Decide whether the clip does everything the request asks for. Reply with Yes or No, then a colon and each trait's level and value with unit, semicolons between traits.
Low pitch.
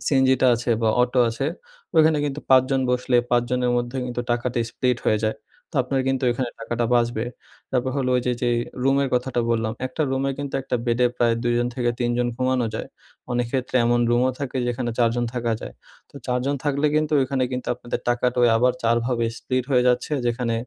Yes: low, 125 Hz